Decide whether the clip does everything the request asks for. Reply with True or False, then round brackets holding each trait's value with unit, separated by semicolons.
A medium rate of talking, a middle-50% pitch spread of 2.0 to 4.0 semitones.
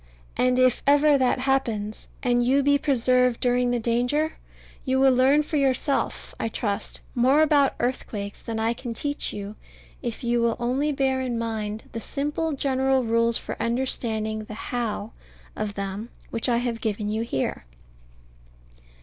True (160 wpm; 3.0 semitones)